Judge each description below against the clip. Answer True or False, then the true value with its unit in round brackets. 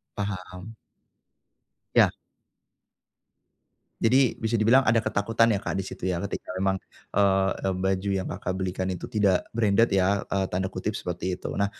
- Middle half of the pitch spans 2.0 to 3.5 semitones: True (2.4 semitones)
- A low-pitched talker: True (95 Hz)